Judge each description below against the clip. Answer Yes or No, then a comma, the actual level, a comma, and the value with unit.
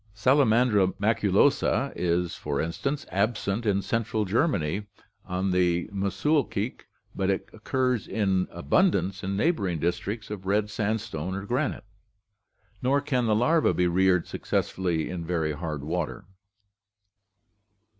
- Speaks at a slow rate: Yes, slow, 125 wpm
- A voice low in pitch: Yes, low, 100 Hz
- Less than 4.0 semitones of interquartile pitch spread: No, average, 4.4 semitones